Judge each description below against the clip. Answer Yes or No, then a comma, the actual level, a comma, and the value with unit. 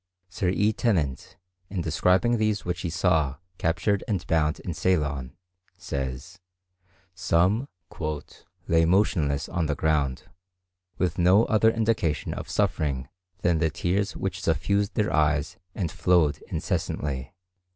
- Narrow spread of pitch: No, average, 4.3 semitones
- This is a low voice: Yes, very low, 85 Hz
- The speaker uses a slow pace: Yes, slow, 125 wpm